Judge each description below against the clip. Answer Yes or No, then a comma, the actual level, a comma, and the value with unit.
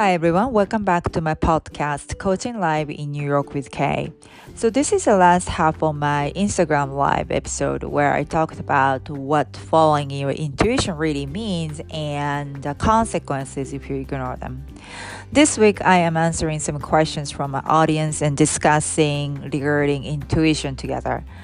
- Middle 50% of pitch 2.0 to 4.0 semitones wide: Yes, average, 2.8 semitones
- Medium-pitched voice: Yes, medium, 150 Hz